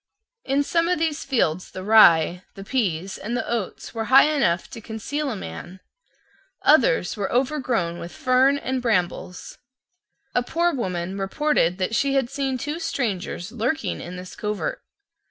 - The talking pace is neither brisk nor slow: Yes, average, 155 wpm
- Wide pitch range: Yes, wide, 6.9 semitones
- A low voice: No, high, 230 Hz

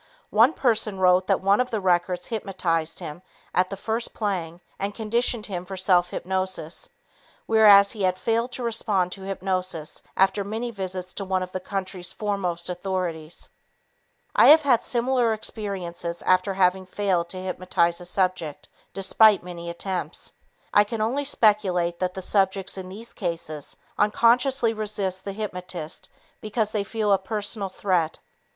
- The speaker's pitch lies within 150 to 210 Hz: Yes, high, 190 Hz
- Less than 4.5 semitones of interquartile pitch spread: Yes, average, 2.9 semitones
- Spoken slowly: No, average, 155 wpm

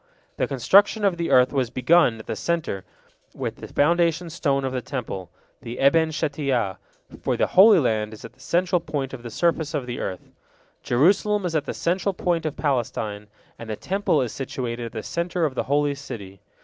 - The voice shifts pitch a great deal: Yes, wide, 5.9 semitones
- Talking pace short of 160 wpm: No, average, 200 wpm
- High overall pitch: No, medium, 140 Hz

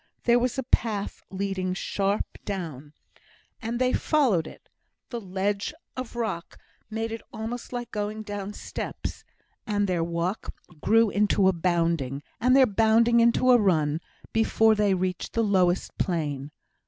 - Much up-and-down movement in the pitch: No, average, 4.0 semitones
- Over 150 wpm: No, average, 145 wpm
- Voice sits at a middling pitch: No, high, 205 Hz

